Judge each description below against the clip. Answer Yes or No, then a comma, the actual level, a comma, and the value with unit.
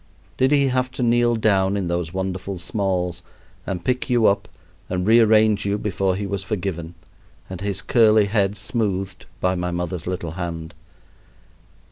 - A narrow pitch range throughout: No, average, 3.2 semitones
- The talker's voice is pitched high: No, very low, 95 Hz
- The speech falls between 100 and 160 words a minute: Yes, average, 155 wpm